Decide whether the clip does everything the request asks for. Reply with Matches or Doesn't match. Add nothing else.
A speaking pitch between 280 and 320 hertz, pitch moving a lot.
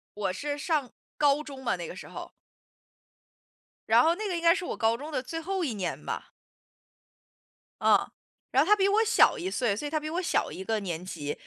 Matches